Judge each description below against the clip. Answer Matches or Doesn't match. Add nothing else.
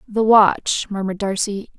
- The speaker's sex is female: Matches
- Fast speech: Doesn't match